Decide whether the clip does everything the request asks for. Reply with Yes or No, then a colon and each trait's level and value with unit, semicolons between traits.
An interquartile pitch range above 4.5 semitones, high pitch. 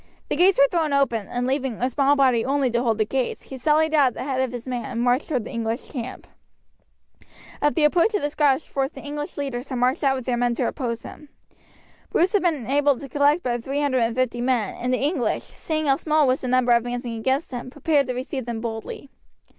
No: average, 3.0 semitones; very high, 260 Hz